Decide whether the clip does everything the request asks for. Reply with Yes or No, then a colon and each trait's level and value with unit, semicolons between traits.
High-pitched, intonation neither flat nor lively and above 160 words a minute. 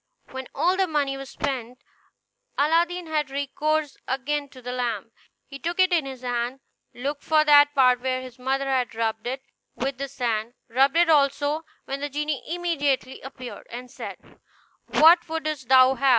Yes: very high, 275 Hz; average, 3.0 semitones; average, 170 wpm